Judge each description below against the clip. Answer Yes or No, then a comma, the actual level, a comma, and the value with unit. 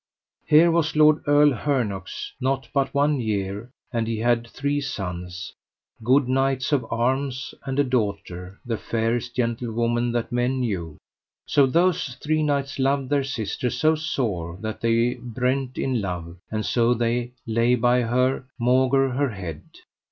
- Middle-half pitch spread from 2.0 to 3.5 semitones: Yes, average, 3.2 semitones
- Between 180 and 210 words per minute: No, average, 150 wpm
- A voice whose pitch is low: Yes, low, 125 Hz